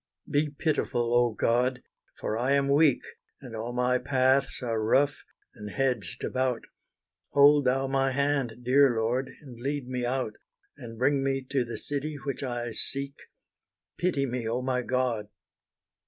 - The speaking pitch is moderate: No, low, 130 Hz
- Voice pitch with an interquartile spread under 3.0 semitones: Yes, narrow, 2.4 semitones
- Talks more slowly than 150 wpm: No, average, 155 wpm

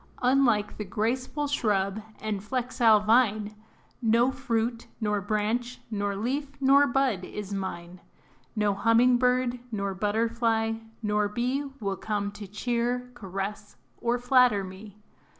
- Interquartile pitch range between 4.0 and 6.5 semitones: No, average, 3.2 semitones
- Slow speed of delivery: Yes, slow, 125 wpm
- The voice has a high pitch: Yes, high, 220 Hz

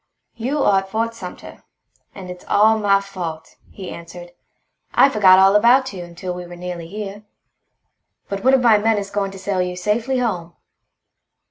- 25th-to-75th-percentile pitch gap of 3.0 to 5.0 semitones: Yes, average, 3.5 semitones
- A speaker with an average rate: Yes, average, 175 wpm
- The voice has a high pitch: Yes, high, 195 Hz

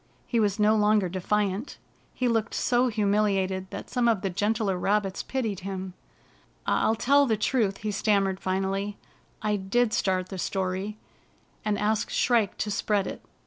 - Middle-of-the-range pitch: No, high, 205 Hz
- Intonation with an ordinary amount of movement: No, narrow, 2.3 semitones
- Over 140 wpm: Yes, average, 165 wpm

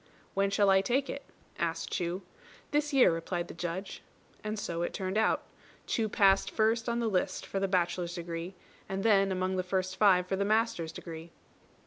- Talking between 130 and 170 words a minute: No, average, 185 wpm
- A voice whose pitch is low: No, high, 190 Hz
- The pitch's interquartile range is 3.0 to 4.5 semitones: Yes, average, 3.3 semitones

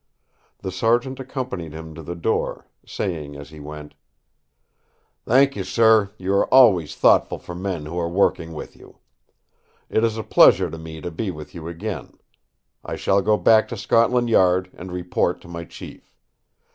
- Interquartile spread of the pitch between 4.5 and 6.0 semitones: Yes, wide, 5.5 semitones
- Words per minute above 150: Yes, average, 170 wpm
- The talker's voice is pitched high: No, very low, 90 Hz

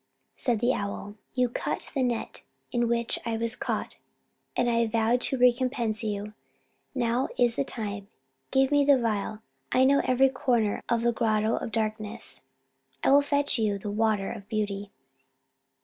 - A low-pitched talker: No, high, 230 Hz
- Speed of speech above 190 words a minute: No, average, 165 wpm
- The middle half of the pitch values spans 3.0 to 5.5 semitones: No, narrow, 2.6 semitones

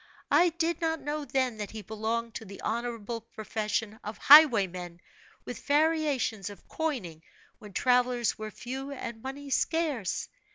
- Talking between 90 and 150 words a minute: Yes, average, 140 wpm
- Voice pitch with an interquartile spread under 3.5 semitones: No, average, 4.9 semitones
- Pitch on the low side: No, high, 235 Hz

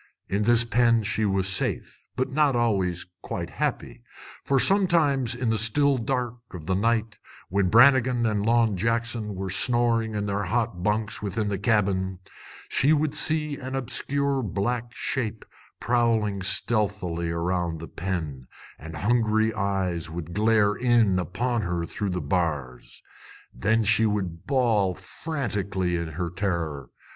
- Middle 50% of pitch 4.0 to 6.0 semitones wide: Yes, average, 4.3 semitones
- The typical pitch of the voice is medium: No, low, 105 Hz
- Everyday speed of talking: Yes, average, 145 wpm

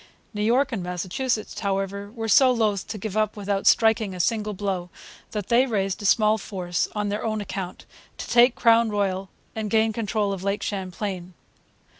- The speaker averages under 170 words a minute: No, average, 180 wpm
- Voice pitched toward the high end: Yes, high, 210 Hz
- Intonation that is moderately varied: No, narrow, 2.3 semitones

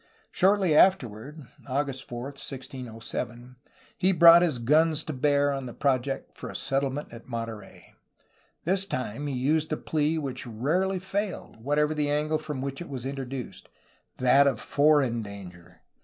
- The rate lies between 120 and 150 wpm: Yes, average, 140 wpm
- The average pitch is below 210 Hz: Yes, medium, 140 Hz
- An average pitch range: Yes, average, 3.7 semitones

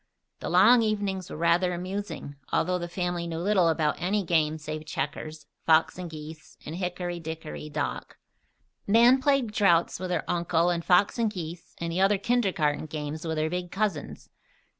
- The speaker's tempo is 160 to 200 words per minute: Yes, average, 170 wpm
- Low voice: No, medium, 175 Hz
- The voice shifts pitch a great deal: No, average, 3.5 semitones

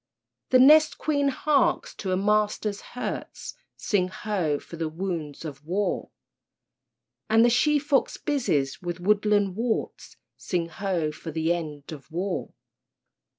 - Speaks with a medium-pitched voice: No, high, 195 Hz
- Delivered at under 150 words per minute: Yes, slow, 135 wpm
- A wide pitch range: Yes, wide, 5.7 semitones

